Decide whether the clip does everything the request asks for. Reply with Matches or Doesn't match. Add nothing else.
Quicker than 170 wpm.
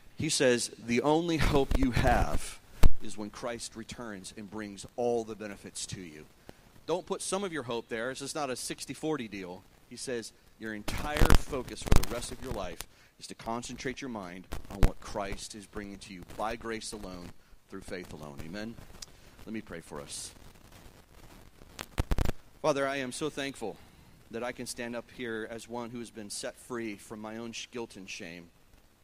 Matches